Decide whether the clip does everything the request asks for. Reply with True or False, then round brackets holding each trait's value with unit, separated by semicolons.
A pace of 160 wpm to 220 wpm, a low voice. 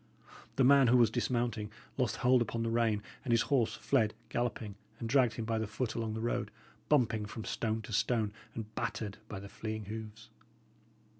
True (190 wpm; 115 Hz)